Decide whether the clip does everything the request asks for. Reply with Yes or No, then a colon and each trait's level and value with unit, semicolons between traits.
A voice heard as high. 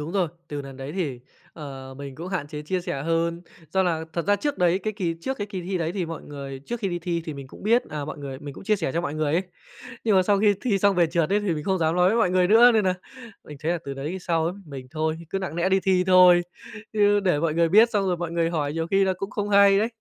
No: medium, 175 Hz